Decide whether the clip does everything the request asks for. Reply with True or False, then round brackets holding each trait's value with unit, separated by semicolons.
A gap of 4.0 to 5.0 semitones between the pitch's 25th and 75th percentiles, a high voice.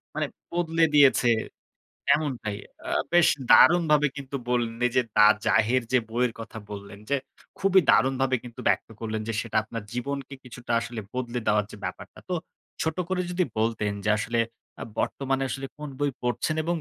False (4.3 semitones; 125 Hz)